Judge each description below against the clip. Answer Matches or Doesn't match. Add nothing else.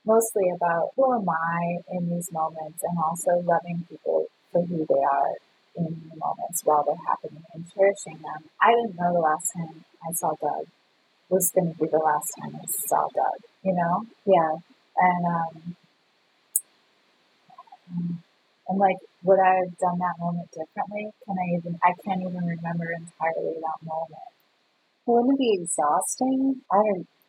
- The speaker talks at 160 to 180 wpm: Matches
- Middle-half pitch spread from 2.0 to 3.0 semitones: Matches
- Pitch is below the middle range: Doesn't match